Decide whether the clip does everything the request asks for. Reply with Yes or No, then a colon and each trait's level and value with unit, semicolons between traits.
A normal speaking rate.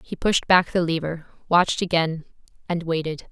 Yes: average, 165 wpm